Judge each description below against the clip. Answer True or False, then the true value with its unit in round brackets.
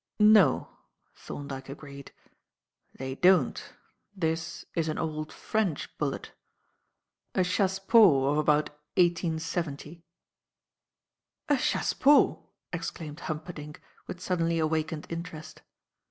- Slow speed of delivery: True (90 wpm)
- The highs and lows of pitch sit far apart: False (3.1 semitones)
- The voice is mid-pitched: True (160 Hz)